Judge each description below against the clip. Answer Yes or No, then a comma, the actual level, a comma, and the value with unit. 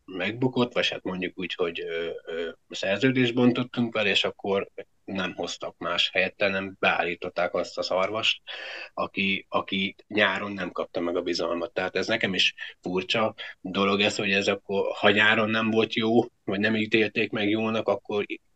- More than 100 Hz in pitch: Yes, low, 110 Hz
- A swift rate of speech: Yes, fast, 160 wpm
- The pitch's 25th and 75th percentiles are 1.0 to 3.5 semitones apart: No, average, 3.9 semitones